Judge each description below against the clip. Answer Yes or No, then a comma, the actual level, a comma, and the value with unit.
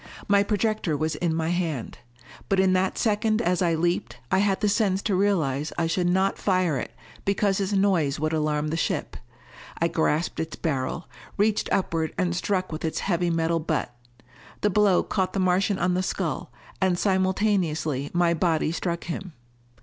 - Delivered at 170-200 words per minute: Yes, average, 175 wpm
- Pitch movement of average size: Yes, average, 3.3 semitones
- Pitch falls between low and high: Yes, medium, 180 Hz